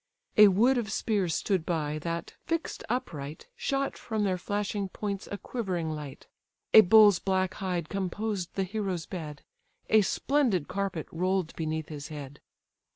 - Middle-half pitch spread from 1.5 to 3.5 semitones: No, average, 4.5 semitones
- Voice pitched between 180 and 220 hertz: Yes, high, 190 Hz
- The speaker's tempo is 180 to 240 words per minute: No, average, 150 wpm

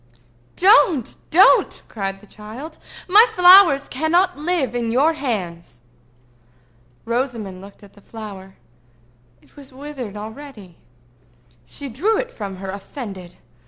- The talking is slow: Yes, slow, 120 wpm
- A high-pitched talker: Yes, high, 245 Hz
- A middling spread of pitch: No, wide, 7.3 semitones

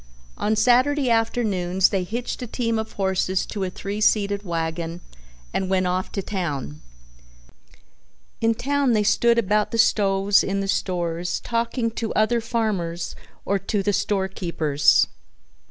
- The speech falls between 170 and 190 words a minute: No, average, 145 wpm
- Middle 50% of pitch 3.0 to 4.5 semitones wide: Yes, average, 3.8 semitones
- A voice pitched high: Yes, high, 200 Hz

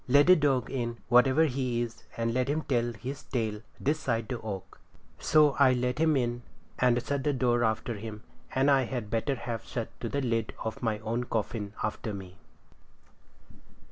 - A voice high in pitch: No, low, 120 Hz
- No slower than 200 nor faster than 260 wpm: No, average, 185 wpm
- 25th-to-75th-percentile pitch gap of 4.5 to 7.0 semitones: No, average, 2.9 semitones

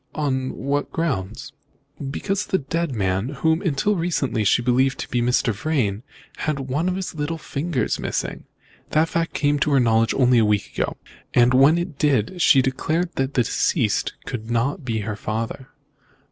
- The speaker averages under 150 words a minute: No, average, 170 wpm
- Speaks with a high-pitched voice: No, low, 135 Hz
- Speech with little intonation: No, average, 5.1 semitones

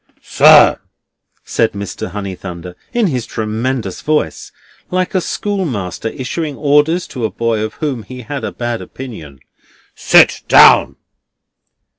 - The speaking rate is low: Yes, slow, 125 wpm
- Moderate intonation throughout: No, wide, 6.0 semitones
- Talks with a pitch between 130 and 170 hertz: No, low, 120 Hz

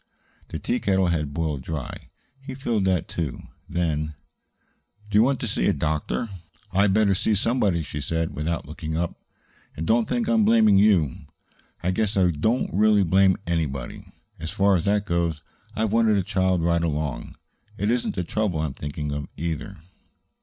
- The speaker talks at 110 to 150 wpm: No, average, 175 wpm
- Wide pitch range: No, average, 4.8 semitones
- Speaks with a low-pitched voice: Yes, very low, 90 Hz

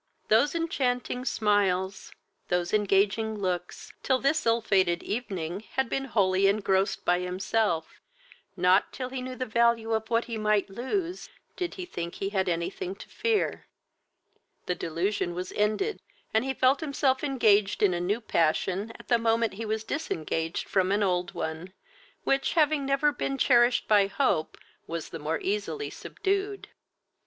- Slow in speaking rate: No, average, 155 wpm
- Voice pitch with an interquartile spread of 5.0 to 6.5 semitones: Yes, wide, 5.5 semitones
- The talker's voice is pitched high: Yes, high, 215 Hz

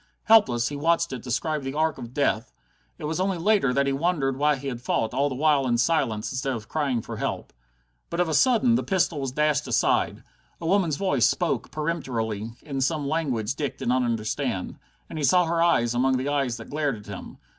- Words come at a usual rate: No, fast, 215 wpm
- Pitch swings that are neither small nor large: Yes, average, 4.6 semitones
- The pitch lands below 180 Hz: Yes, medium, 140 Hz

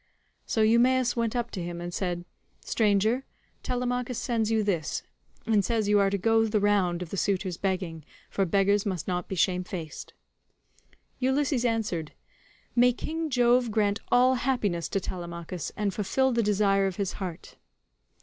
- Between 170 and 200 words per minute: No, average, 160 wpm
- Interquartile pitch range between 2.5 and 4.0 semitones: No, average, 4.4 semitones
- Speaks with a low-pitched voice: No, high, 205 Hz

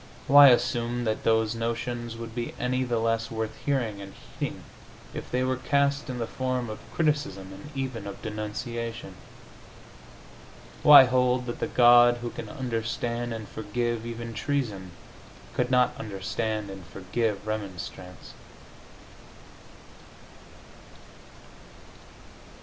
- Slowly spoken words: Yes, slow, 120 wpm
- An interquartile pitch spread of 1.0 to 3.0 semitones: Yes, narrow, 2.4 semitones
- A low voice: Yes, low, 115 Hz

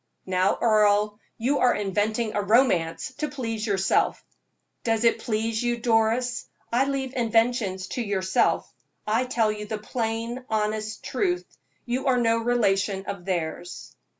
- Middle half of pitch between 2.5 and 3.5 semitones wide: Yes, average, 2.9 semitones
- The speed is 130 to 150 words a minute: Yes, average, 140 wpm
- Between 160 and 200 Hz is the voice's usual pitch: No, high, 225 Hz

